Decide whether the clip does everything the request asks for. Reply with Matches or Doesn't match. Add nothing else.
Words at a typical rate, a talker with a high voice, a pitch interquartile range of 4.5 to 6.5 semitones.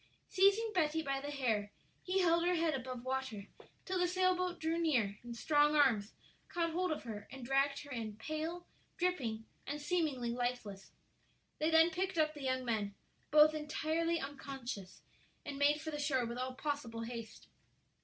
Matches